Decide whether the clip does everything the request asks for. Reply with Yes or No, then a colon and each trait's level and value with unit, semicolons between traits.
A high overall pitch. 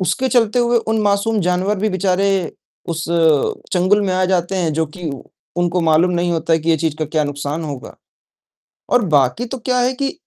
No: medium, 180 Hz